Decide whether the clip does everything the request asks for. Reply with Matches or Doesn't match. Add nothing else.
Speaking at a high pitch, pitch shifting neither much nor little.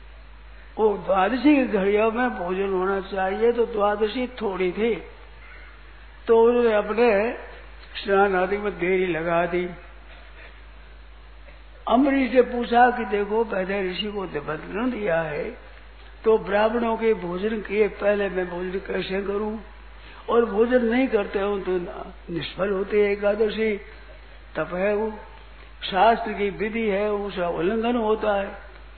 Matches